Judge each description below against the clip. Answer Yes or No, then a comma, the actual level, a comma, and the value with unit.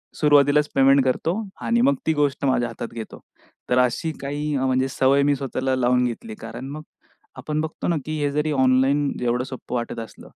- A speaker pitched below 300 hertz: Yes, low, 135 Hz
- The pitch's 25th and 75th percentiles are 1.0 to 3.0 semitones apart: Yes, average, 2.7 semitones